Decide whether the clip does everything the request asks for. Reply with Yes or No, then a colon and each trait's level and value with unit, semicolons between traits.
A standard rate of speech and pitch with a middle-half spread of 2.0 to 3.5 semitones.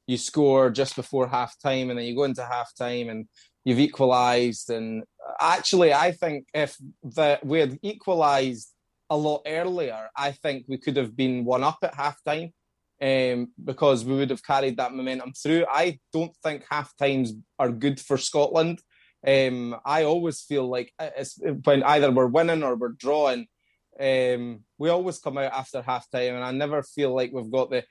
Yes: average, 185 wpm; average, 2.9 semitones